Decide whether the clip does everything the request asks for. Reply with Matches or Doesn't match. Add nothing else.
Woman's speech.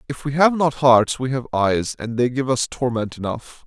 Doesn't match